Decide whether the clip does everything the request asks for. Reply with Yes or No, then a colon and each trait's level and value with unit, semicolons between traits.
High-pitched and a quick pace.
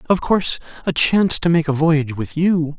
No: medium, 160 Hz; fast, 215 wpm